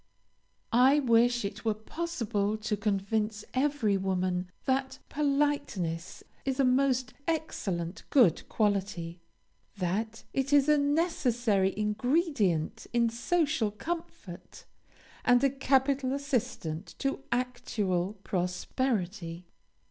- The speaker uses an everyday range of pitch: No, wide, 5.7 semitones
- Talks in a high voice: Yes, high, 235 Hz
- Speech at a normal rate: No, slow, 100 wpm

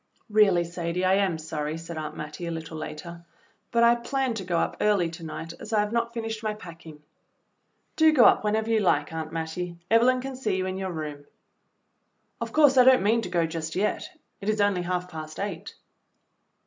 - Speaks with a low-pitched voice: No, medium, 185 Hz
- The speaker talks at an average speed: No, fast, 210 wpm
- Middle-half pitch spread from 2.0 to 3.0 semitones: No, average, 5.1 semitones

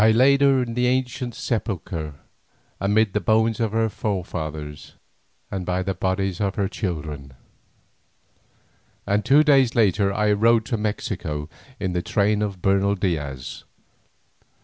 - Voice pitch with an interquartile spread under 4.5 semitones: Yes, average, 4.0 semitones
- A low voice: Yes, low, 100 Hz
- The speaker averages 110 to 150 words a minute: Yes, average, 140 wpm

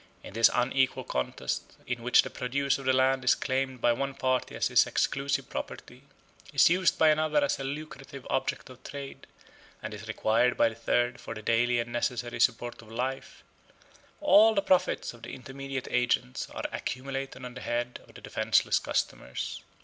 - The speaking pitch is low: Yes, low, 130 Hz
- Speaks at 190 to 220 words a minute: No, average, 180 wpm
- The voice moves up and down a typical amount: No, narrow, 2.3 semitones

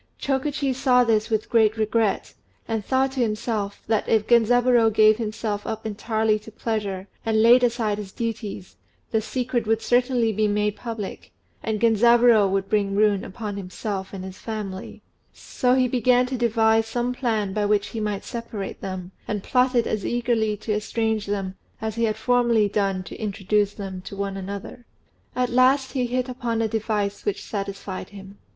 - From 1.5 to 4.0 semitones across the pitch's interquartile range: Yes, average, 2.7 semitones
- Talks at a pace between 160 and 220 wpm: Yes, average, 170 wpm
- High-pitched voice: Yes, high, 220 Hz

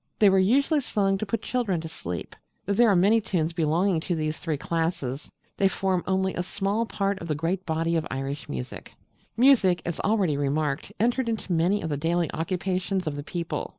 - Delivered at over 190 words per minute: Yes, average, 200 wpm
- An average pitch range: Yes, average, 3.8 semitones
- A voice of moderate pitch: Yes, medium, 180 Hz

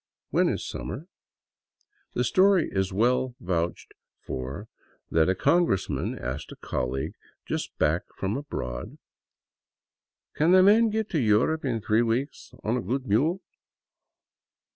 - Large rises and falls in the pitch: Yes, wide, 8.9 semitones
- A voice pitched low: Yes, low, 115 Hz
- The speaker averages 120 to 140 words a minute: Yes, slow, 135 wpm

